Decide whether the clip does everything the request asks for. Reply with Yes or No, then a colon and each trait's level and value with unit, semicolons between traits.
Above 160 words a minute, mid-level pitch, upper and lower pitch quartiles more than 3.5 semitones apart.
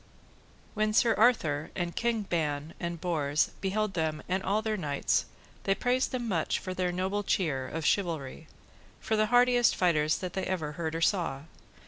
Yes: average, 170 wpm; medium, 180 Hz; average, 5.2 semitones